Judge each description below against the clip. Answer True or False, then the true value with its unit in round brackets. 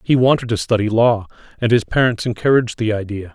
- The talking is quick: False (195 wpm)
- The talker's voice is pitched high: False (110 Hz)